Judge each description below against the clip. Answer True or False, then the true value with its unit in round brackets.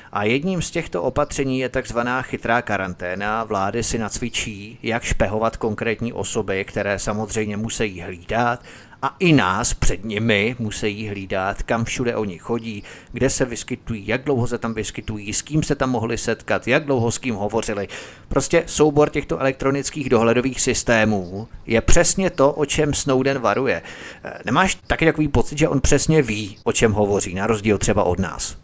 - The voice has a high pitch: False (115 Hz)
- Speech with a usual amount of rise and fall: True (4.0 semitones)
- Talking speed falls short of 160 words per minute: False (165 wpm)